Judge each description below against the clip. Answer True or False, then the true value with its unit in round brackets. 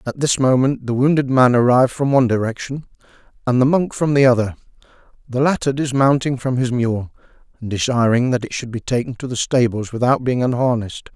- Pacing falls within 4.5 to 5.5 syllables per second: False (5.9 syllables/s)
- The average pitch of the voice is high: False (125 Hz)